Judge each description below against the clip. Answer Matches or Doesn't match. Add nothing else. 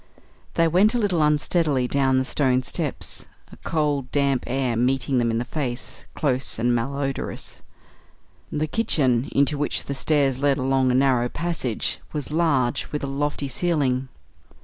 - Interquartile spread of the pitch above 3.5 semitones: Doesn't match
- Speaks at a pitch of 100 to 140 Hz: Matches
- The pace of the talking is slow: Doesn't match